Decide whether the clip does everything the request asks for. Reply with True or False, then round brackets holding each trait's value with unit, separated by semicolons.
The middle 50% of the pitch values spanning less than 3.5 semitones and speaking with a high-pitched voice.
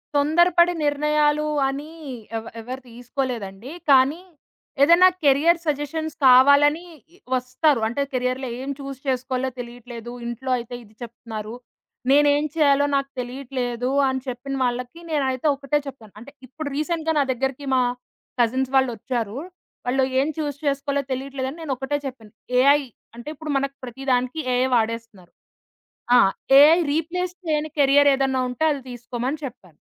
True (2.9 semitones; 270 Hz)